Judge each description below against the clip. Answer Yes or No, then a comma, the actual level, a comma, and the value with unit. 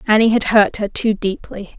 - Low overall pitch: No, high, 210 Hz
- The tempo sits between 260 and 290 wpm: No, average, 200 wpm